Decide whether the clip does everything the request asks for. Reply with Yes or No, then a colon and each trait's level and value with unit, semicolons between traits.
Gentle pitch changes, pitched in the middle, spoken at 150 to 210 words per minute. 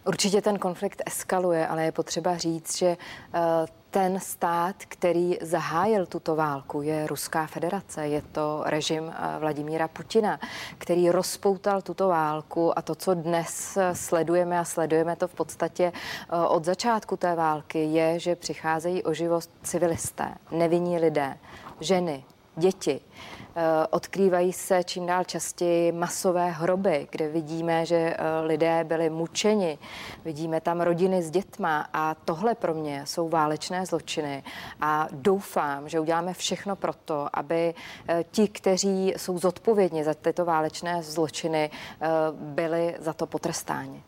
No: narrow, 2.2 semitones; medium, 170 Hz; average, 130 wpm